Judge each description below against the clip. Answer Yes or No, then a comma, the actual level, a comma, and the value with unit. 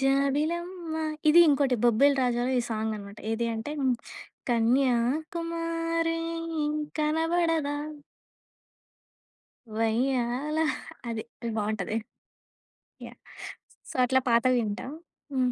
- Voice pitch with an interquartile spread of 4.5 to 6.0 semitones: Yes, average, 5.2 semitones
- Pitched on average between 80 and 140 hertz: No, very high, 270 Hz